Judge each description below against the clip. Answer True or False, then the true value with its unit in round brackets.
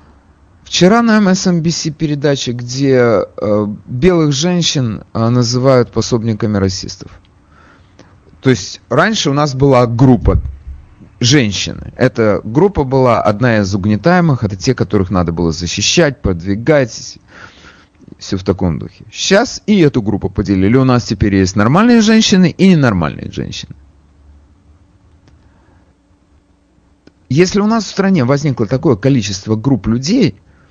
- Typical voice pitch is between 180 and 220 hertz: False (115 Hz)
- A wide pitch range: True (7.2 semitones)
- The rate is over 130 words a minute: False (120 wpm)